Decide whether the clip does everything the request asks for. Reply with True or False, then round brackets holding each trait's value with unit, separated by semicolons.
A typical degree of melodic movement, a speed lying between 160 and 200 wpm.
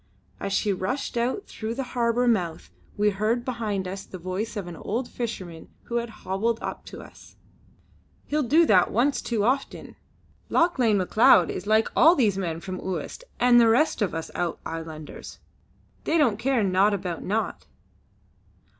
True (4.4 semitones; 165 wpm)